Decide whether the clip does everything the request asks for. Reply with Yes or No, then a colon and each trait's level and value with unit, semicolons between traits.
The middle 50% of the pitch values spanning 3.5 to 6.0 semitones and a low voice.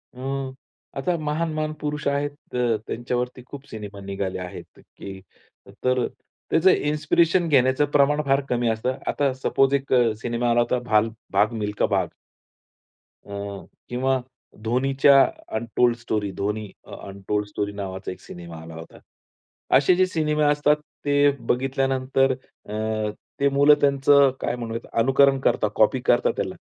Yes: average, 4.2 semitones; low, 130 Hz